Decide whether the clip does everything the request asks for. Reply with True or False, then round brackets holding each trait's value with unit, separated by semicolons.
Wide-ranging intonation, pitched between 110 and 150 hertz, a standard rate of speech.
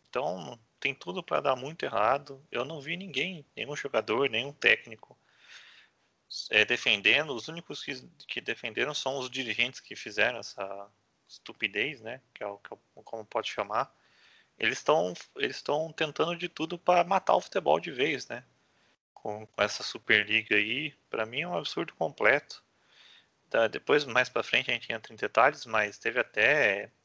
True (6.2 semitones; 140 Hz; 175 wpm)